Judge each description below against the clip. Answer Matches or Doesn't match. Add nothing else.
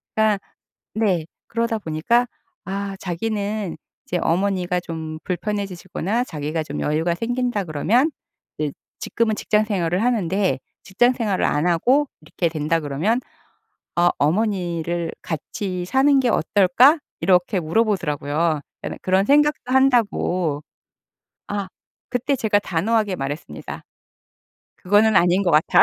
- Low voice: Doesn't match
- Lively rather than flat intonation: Doesn't match